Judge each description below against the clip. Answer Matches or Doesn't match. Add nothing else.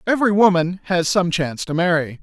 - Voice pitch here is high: Doesn't match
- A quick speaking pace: Doesn't match